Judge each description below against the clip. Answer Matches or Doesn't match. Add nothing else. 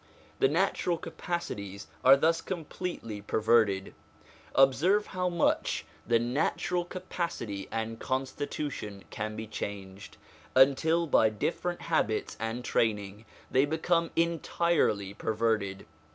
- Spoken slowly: Matches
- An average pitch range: Doesn't match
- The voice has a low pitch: Matches